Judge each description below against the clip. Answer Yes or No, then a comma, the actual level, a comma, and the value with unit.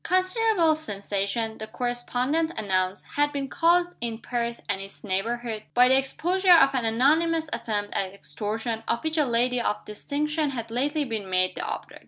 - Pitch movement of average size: No, wide, 5.8 semitones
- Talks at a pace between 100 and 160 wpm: No, average, 170 wpm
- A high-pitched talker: Yes, high, 245 Hz